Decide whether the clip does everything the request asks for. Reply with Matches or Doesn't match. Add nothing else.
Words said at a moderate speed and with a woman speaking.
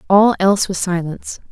Matches